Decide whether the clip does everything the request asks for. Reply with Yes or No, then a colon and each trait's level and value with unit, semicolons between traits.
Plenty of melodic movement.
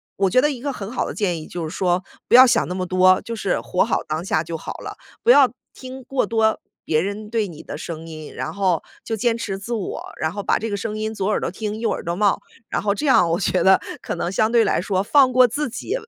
No: average, 4.3 semitones